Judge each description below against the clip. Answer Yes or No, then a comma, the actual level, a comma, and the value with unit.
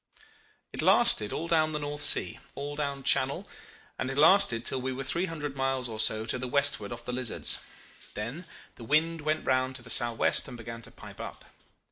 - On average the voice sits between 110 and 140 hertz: Yes, low, 135 Hz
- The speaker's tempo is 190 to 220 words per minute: Yes, average, 200 wpm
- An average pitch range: Yes, average, 3.6 semitones